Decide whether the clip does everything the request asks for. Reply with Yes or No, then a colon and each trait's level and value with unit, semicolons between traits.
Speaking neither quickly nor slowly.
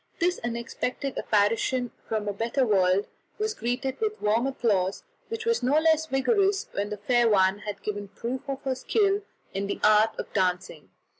Yes: average, 170 wpm